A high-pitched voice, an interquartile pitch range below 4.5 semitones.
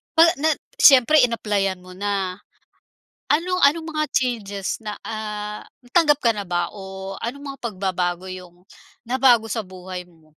No: high, 210 Hz; wide, 5.6 semitones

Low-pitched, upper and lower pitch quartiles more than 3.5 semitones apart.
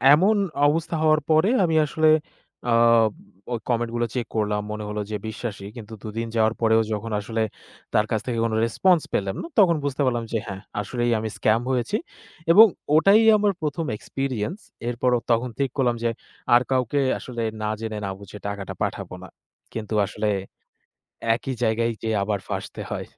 Yes: low, 120 Hz; average, 4.7 semitones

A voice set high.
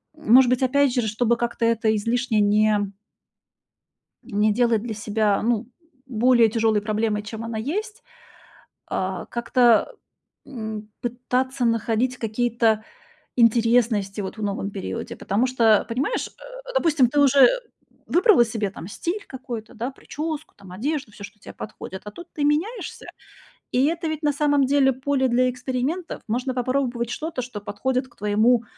Yes: high, 240 Hz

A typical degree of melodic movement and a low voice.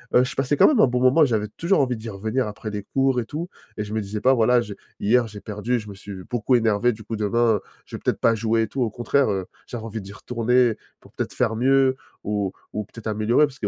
Yes: average, 3.0 semitones; low, 115 Hz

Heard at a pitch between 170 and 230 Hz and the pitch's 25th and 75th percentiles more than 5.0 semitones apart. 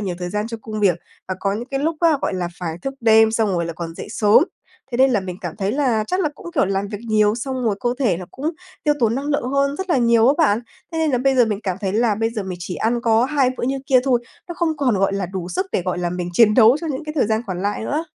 Yes: high, 225 Hz; wide, 5.6 semitones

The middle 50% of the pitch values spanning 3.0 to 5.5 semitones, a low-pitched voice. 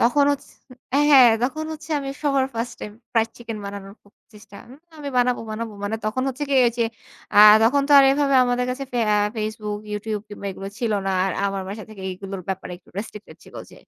No: average, 4.0 semitones; high, 225 Hz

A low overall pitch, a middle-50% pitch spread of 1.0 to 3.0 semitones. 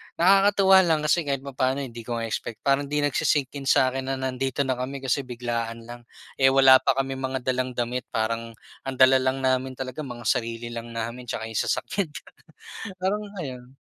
Yes: low, 130 Hz; narrow, 2.4 semitones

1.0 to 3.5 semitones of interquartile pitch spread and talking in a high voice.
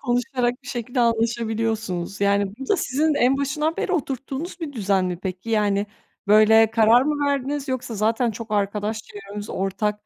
No: average, 4.3 semitones; high, 225 Hz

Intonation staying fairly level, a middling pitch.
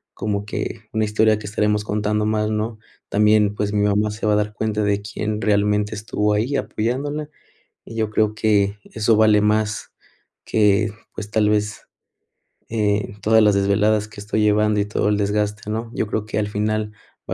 No: narrow, 0.7 semitones; low, 105 Hz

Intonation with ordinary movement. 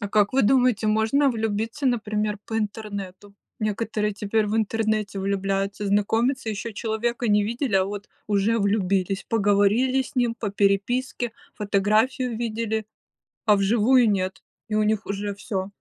No: narrow, 2.3 semitones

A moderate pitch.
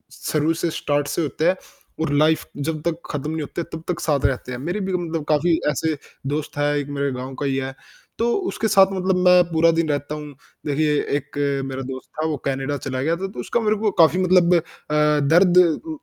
Yes: medium, 155 Hz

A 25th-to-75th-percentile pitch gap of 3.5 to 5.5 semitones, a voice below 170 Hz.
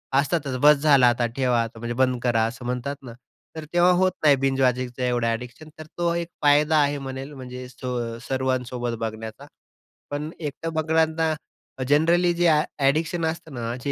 Yes: average, 4.2 semitones; low, 135 Hz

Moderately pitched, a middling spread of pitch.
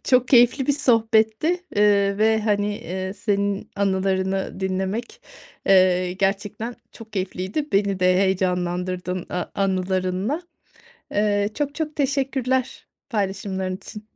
No: high, 200 Hz; average, 3.5 semitones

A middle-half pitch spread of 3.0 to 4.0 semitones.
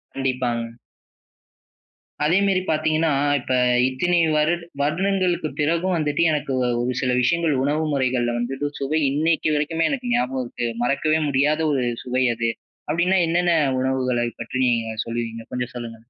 No: average, 4.7 semitones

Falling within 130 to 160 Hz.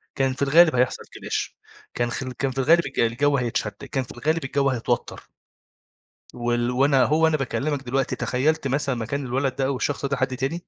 Yes: low, 135 Hz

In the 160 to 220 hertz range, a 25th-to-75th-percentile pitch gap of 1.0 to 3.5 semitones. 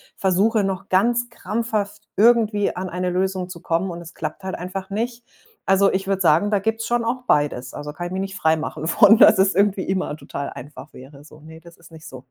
No: high, 190 Hz; average, 3.9 semitones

